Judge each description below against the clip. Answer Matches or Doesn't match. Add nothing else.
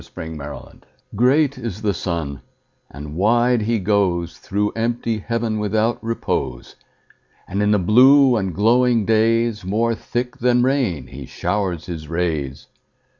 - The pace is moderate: Doesn't match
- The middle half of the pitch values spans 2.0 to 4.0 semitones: Doesn't match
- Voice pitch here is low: Matches